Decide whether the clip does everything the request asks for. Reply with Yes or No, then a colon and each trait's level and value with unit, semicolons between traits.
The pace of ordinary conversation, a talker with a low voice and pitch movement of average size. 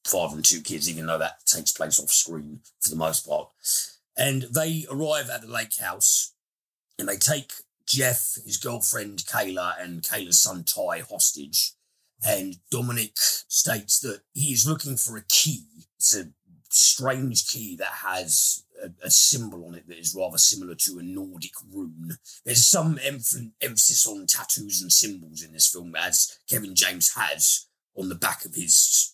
No: average, 170 wpm; low, 105 Hz; wide, 7.6 semitones